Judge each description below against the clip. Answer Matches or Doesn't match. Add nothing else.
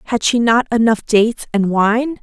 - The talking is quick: Doesn't match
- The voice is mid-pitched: Doesn't match